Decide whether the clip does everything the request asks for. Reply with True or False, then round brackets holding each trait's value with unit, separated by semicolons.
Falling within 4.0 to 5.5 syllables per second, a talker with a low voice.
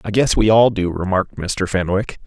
True (5.3 syllables/s; 100 Hz)